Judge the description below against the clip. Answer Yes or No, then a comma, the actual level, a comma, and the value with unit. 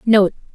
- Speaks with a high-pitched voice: Yes, high, 210 Hz